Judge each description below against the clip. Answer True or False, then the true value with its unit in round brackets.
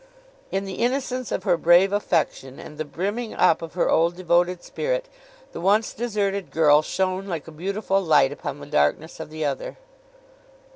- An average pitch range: True (4.0 semitones)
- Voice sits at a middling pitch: True (180 Hz)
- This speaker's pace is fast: False (175 wpm)